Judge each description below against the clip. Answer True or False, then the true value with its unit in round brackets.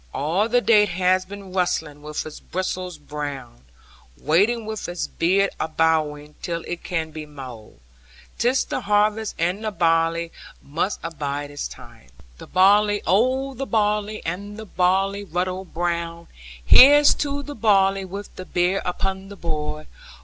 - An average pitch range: True (4.3 semitones)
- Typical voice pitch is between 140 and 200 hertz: True (185 Hz)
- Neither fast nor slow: True (155 wpm)